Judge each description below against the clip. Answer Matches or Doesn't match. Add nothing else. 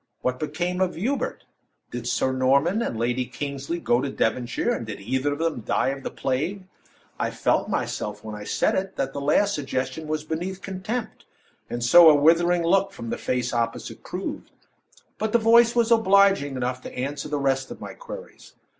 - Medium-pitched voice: Matches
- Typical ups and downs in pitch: Doesn't match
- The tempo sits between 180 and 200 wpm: Matches